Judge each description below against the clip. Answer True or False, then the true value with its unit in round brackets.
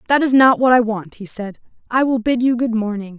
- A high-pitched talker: True (235 Hz)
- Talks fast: True (265 wpm)